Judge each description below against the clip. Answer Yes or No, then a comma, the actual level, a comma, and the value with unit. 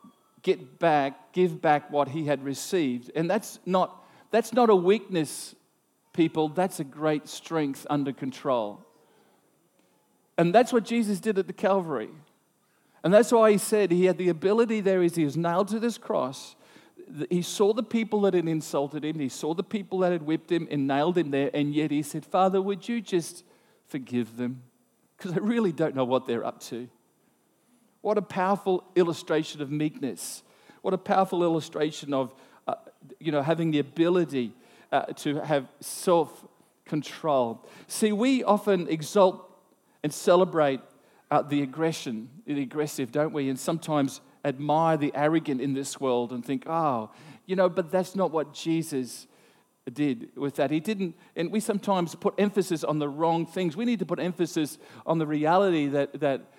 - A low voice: No, medium, 165 Hz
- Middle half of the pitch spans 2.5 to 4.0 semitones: No, average, 4.7 semitones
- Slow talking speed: No, average, 170 wpm